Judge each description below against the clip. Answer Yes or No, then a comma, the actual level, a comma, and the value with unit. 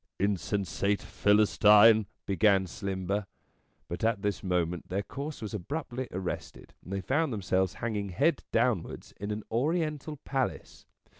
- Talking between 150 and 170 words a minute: No, slow, 135 wpm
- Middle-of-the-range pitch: No, low, 105 Hz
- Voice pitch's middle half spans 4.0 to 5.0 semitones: Yes, average, 4.4 semitones